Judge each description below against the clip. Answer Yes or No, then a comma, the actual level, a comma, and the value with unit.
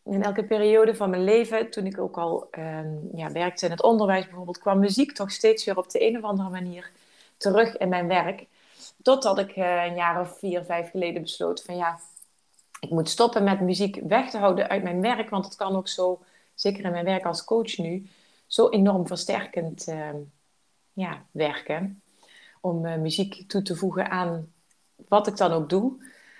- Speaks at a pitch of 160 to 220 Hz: Yes, high, 190 Hz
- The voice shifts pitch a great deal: No, average, 2.7 semitones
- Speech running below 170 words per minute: No, average, 195 wpm